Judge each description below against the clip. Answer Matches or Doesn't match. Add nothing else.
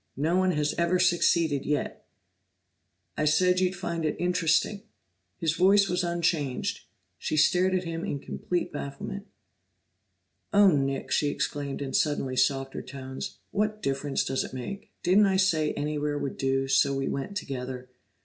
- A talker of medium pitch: Matches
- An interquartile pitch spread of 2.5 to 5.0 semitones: Matches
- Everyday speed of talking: Matches